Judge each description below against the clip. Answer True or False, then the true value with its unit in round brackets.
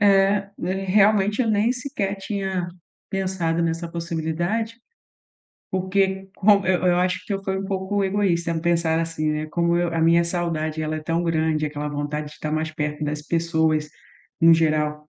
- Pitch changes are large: False (3.5 semitones)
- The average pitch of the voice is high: False (170 Hz)